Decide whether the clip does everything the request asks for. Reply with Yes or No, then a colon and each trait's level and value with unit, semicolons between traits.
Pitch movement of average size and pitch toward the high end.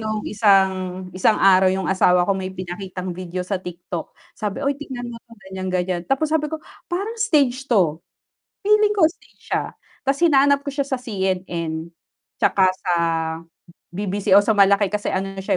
No: wide, 6.5 semitones; high, 195 Hz